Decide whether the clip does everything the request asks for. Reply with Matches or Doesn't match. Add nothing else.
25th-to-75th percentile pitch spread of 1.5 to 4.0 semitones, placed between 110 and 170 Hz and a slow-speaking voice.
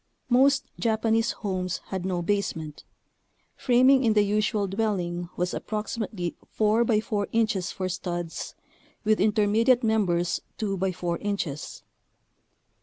Doesn't match